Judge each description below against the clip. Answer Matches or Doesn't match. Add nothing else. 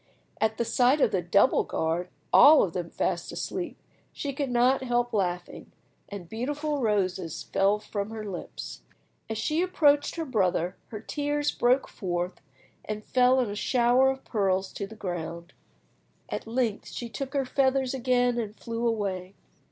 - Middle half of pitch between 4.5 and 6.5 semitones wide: Matches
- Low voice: Doesn't match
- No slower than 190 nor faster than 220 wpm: Doesn't match